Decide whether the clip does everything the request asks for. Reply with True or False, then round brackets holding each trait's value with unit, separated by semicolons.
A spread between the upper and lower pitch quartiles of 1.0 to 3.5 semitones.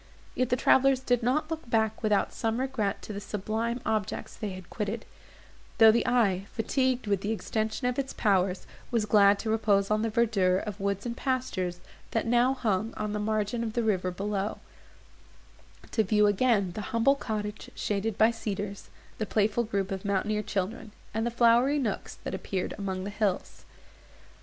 True (2.7 semitones)